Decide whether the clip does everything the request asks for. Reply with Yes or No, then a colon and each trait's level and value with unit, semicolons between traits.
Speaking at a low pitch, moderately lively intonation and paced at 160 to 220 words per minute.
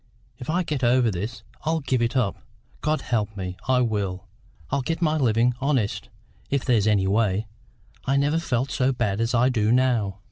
Yes: low, 120 Hz; average, 4.2 semitones; average, 185 wpm